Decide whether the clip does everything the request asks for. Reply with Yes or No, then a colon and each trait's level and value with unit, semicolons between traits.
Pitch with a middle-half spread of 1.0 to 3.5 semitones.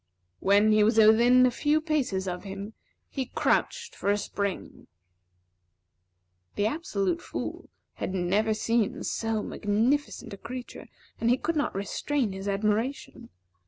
No: average, 4.0 semitones